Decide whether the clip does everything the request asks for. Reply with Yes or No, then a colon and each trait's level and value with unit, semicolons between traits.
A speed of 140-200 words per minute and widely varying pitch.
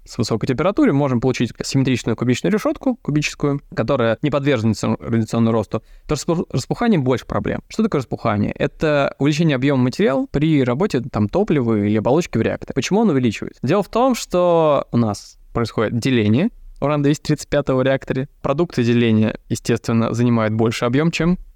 No: average, 155 wpm; average, 5.0 semitones